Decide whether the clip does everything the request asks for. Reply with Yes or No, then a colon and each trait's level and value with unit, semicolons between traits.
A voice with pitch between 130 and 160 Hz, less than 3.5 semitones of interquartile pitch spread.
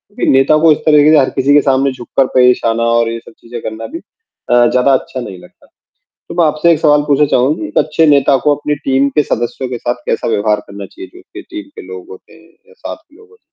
No: low, 135 Hz; average, 4.2 semitones